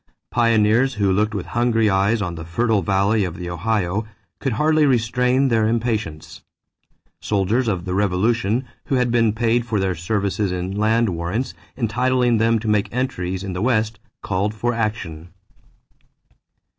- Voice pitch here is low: Yes, low, 110 Hz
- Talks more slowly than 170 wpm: Yes, average, 155 wpm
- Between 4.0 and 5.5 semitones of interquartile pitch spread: No, average, 3.6 semitones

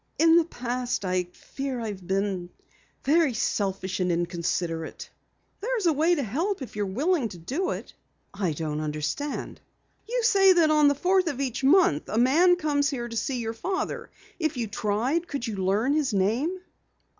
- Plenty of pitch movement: Yes, wide, 8.7 semitones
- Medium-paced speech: Yes, average, 175 wpm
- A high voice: Yes, very high, 255 Hz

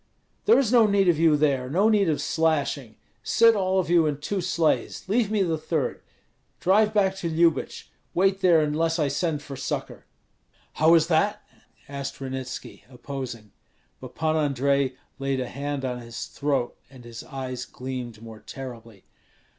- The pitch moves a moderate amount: Yes, average, 5.0 semitones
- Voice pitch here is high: No, medium, 150 Hz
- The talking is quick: No, average, 165 wpm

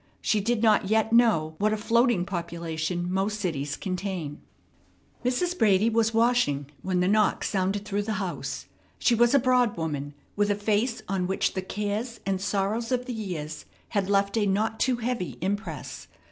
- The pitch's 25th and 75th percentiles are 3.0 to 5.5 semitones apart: Yes, average, 3.8 semitones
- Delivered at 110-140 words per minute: No, average, 175 wpm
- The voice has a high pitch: Yes, high, 205 Hz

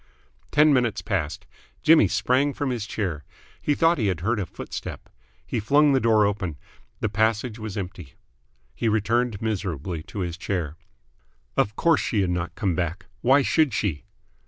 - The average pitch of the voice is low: Yes, low, 105 Hz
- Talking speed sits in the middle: Yes, average, 165 wpm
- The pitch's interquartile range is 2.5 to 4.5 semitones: No, average, 5.3 semitones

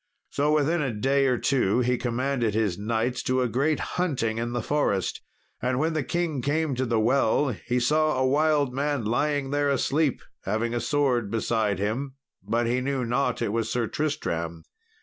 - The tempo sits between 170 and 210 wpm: Yes, average, 190 wpm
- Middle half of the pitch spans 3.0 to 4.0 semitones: Yes, average, 3.7 semitones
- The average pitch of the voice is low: Yes, low, 125 Hz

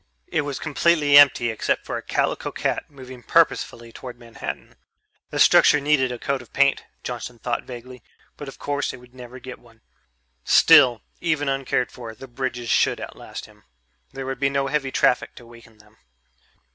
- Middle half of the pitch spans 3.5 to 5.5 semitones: No, narrow, 2.6 semitones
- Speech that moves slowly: No, average, 175 wpm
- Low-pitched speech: Yes, low, 130 Hz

